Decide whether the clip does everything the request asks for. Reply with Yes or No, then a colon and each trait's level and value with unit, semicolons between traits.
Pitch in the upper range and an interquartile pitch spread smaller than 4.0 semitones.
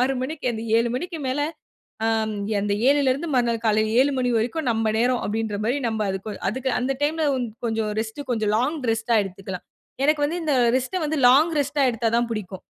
No: high, 240 Hz; average, 4.5 semitones